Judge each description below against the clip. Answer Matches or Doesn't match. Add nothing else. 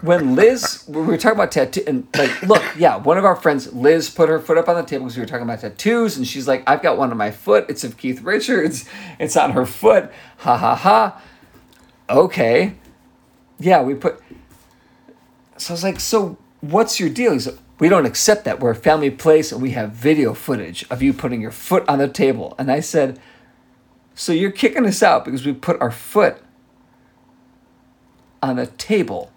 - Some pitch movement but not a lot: Doesn't match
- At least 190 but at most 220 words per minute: Matches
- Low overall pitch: Doesn't match